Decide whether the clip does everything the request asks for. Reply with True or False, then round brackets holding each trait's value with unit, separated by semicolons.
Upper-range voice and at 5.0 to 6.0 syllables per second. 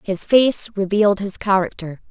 False (200 Hz; 4.8 syllables/s)